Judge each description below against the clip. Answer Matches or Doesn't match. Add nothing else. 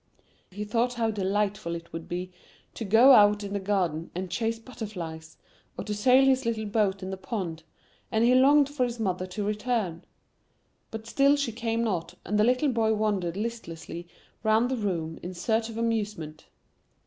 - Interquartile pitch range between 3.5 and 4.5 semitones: Matches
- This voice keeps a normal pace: Matches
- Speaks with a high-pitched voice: Matches